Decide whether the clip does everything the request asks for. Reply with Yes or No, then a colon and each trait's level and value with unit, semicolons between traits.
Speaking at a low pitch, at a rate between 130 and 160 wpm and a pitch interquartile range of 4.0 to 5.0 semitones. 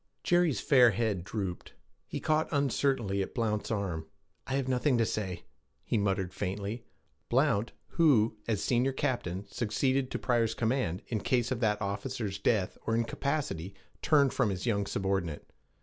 Yes: low, 115 Hz; average, 150 wpm; average, 4.7 semitones